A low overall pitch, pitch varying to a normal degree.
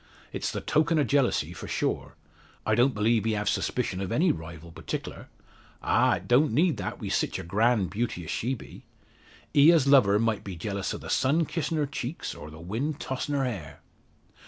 No: low, 120 Hz; wide, 6.3 semitones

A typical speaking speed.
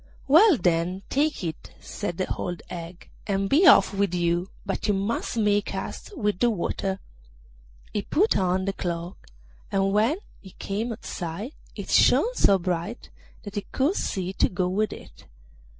Yes: average, 165 wpm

